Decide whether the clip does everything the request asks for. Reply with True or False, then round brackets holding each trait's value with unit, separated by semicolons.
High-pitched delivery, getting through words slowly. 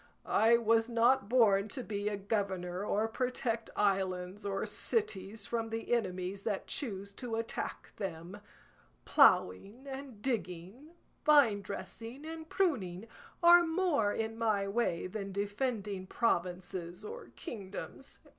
True (215 Hz; 120 wpm)